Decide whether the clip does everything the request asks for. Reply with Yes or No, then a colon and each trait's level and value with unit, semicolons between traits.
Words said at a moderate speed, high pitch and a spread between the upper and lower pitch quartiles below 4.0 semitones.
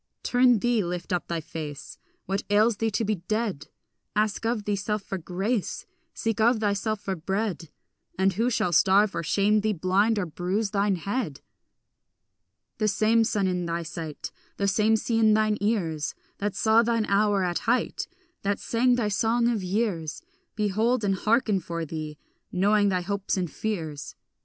Yes: average, 165 wpm; high, 205 Hz; average, 3.3 semitones